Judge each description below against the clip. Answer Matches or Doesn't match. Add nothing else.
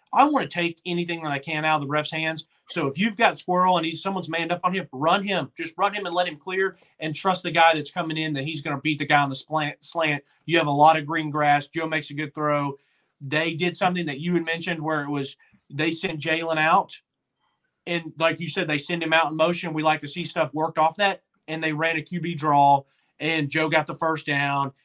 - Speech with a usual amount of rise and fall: Doesn't match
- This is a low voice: Doesn't match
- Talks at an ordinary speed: Doesn't match